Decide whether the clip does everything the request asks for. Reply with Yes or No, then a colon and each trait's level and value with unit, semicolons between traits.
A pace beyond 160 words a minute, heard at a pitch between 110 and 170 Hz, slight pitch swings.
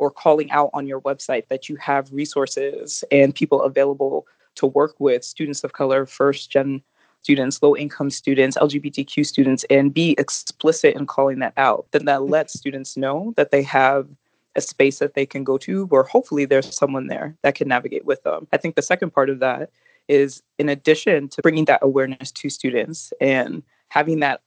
Yes: average, 190 wpm; medium, 140 Hz; narrow, 1.9 semitones